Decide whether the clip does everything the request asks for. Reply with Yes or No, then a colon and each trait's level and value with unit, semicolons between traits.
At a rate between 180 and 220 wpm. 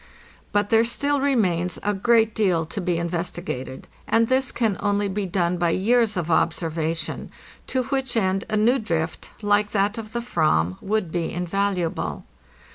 No: average, 160 wpm